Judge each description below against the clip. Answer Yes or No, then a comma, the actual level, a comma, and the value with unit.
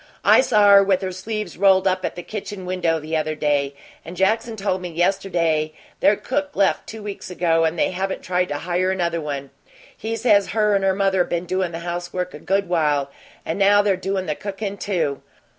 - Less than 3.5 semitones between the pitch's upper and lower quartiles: Yes, average, 3.1 semitones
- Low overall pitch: No, medium, 185 Hz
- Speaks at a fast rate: Yes, fast, 210 wpm